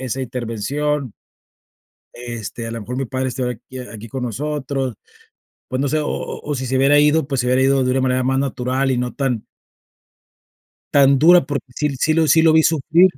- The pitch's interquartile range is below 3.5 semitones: Yes, average, 2.9 semitones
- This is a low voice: Yes, low, 130 Hz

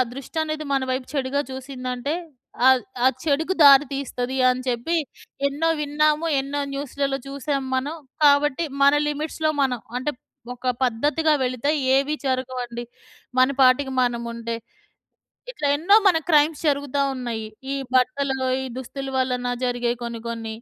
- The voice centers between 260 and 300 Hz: Yes, very high, 270 Hz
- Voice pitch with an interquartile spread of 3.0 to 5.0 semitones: No, narrow, 2.6 semitones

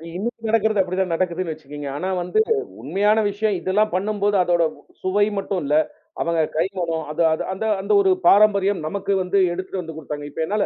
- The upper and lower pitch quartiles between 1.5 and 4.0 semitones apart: Yes, average, 3.4 semitones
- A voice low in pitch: No, medium, 185 Hz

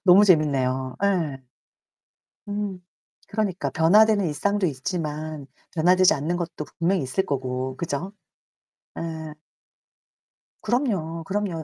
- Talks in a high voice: No, medium, 165 Hz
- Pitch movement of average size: Yes, average, 4.8 semitones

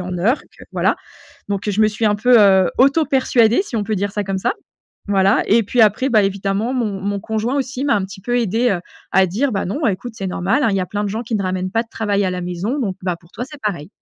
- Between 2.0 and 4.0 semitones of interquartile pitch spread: Yes, average, 3.7 semitones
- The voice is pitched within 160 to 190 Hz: No, high, 205 Hz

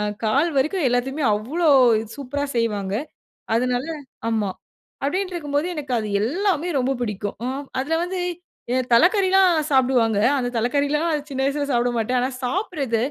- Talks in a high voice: Yes, very high, 270 Hz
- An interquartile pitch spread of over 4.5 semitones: Yes, average, 4.9 semitones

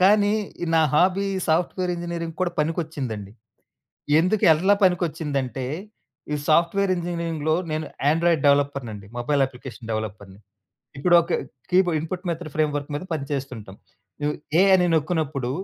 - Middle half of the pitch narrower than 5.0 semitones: Yes, average, 3.9 semitones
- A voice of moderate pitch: Yes, medium, 155 Hz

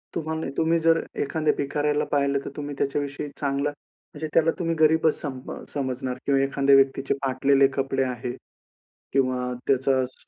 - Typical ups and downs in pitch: No, narrow, 1.9 semitones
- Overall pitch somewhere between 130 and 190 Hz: Yes, medium, 140 Hz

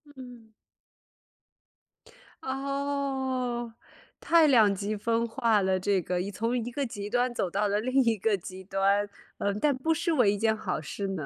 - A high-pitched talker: Yes, high, 230 Hz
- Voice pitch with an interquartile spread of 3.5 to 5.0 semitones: Yes, average, 4.5 semitones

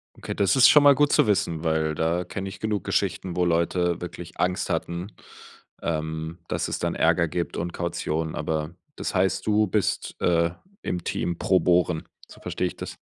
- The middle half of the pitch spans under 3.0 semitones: Yes, narrow, 2.6 semitones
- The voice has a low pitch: Yes, very low, 85 Hz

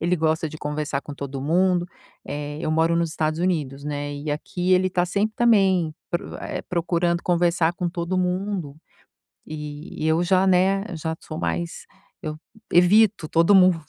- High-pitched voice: No, medium, 170 Hz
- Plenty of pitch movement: No, average, 3.2 semitones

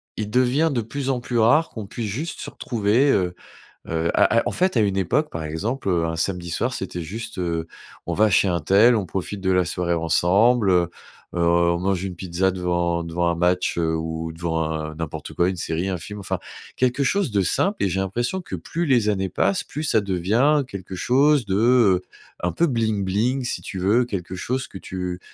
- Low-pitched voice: Yes, very low, 95 Hz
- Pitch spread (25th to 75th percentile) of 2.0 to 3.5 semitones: No, wide, 5.6 semitones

